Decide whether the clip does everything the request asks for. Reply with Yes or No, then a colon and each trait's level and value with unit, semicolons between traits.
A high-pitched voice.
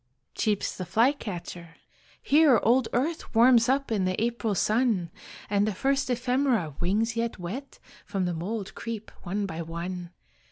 Yes: high, 220 Hz